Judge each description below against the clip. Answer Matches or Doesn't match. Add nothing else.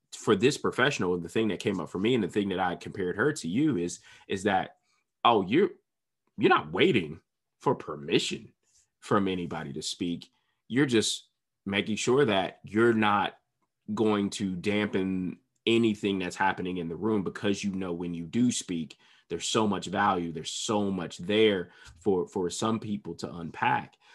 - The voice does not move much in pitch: Doesn't match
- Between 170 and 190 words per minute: Matches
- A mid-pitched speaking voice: Doesn't match